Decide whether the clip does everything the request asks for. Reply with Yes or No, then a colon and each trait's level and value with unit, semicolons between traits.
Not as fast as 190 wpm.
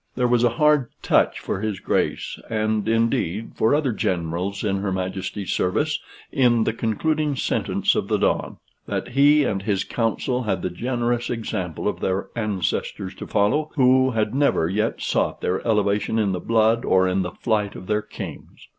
Yes: average, 175 wpm